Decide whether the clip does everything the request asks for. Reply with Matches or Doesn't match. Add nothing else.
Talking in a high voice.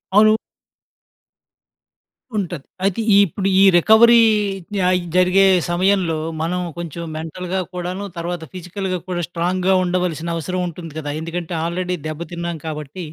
Doesn't match